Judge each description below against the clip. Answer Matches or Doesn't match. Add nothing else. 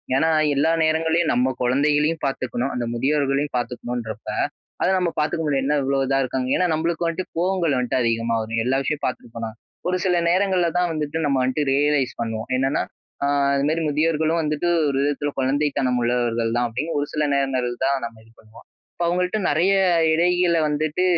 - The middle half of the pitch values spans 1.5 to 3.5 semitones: Doesn't match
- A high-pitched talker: Doesn't match